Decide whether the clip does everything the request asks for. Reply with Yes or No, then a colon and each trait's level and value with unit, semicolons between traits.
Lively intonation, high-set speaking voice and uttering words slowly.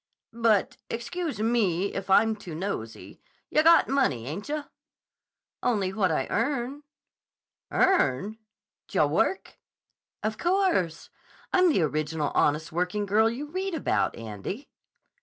Yes: wide, 9.0 semitones; high, 215 Hz; slow, 120 wpm